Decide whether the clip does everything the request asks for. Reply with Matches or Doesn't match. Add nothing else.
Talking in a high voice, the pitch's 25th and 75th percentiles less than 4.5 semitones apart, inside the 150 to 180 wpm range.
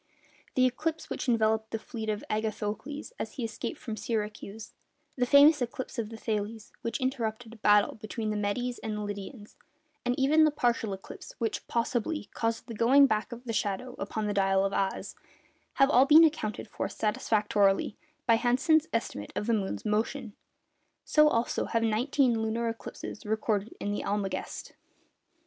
Matches